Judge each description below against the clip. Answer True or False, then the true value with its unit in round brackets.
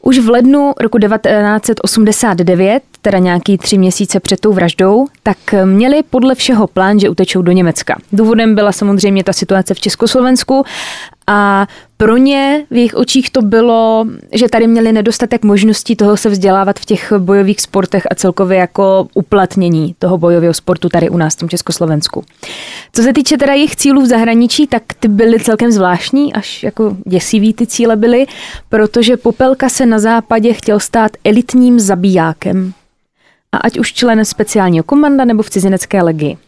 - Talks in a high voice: True (215 Hz)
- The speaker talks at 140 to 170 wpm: True (165 wpm)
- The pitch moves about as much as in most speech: True (3.7 semitones)